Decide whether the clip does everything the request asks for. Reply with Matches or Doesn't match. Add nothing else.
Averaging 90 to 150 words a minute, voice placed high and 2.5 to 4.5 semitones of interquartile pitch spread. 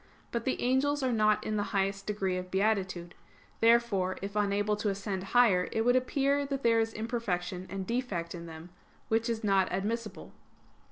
Doesn't match